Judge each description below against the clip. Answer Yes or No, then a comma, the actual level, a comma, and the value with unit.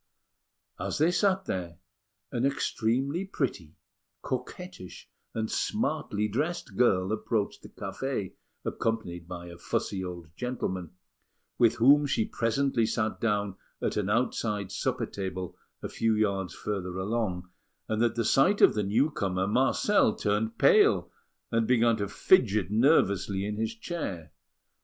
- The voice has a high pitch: No, low, 110 Hz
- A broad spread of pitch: No, average, 5.0 semitones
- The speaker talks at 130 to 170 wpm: Yes, slow, 135 wpm